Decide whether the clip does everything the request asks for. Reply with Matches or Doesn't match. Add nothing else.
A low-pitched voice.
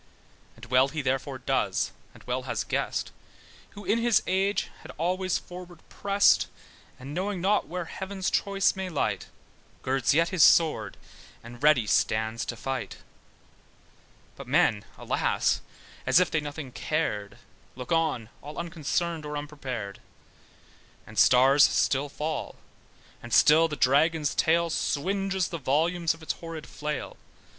Doesn't match